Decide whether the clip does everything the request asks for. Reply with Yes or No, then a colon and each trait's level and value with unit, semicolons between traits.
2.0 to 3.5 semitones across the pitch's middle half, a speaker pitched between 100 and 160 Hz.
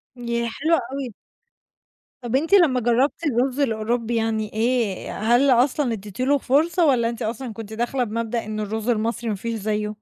No: average, 3.0 semitones; high, 235 Hz